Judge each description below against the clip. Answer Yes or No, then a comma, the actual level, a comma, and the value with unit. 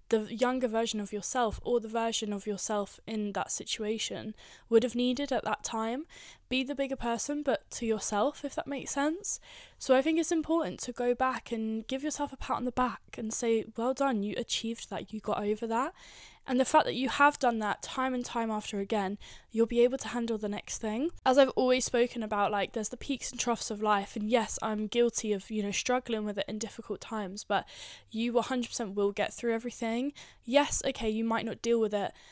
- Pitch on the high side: Yes, high, 230 Hz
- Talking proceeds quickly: Yes, fast, 220 wpm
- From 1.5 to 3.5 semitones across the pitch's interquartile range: Yes, average, 3.1 semitones